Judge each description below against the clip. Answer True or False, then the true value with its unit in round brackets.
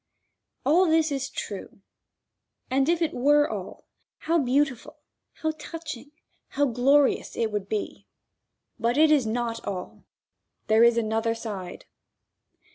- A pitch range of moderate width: True (5.0 semitones)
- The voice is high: True (265 Hz)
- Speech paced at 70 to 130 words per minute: True (125 wpm)